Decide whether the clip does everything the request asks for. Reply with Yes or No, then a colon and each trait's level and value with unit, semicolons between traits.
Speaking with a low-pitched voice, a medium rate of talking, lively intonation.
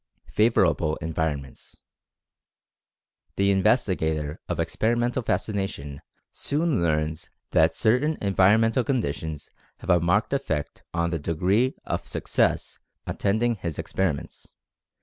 No: very low, 95 Hz; slow, 100 wpm; wide, 6.0 semitones